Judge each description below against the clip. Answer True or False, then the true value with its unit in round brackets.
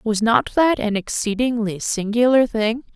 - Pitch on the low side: False (225 Hz)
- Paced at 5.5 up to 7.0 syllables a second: False (4.3 syllables/s)